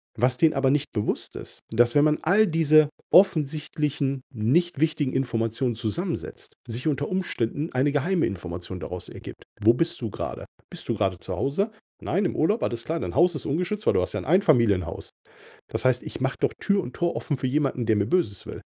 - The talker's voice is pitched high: No, medium, 140 Hz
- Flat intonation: No, wide, 5.8 semitones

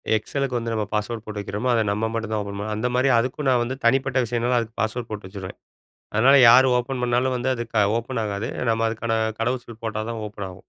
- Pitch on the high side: No, low, 115 Hz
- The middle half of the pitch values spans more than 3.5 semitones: No, narrow, 2.5 semitones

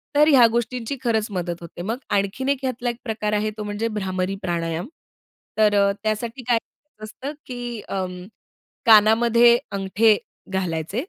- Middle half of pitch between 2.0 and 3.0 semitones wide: No, average, 3.7 semitones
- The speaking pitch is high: Yes, high, 215 Hz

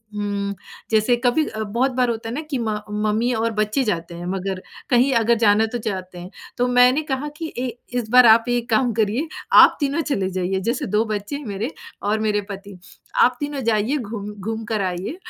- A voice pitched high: Yes, high, 220 Hz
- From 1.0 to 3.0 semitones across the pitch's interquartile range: No, average, 3.5 semitones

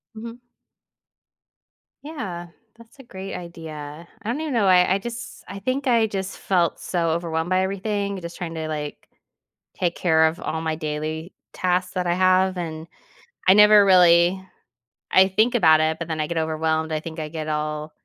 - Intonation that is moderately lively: Yes, average, 3.7 semitones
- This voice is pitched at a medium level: Yes, medium, 175 Hz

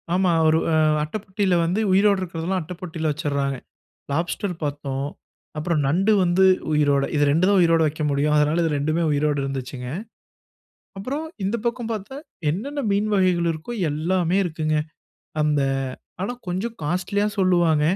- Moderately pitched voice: Yes, medium, 170 Hz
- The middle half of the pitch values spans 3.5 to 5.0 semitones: Yes, average, 4.1 semitones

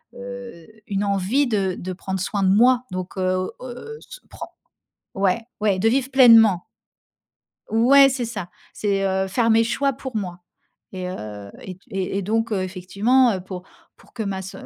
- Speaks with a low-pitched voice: No, high, 200 Hz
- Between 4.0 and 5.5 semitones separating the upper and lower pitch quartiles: Yes, average, 4.5 semitones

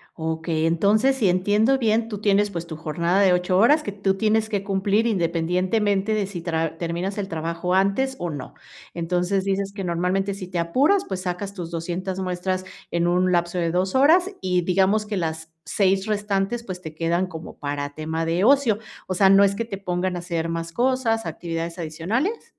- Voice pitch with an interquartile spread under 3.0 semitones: No, average, 3.3 semitones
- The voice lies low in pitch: No, medium, 185 Hz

